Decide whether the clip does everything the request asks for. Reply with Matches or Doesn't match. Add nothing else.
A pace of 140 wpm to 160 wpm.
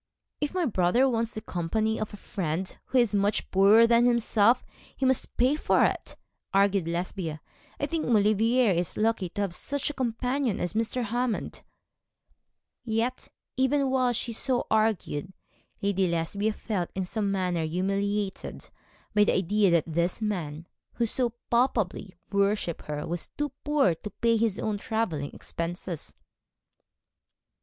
Matches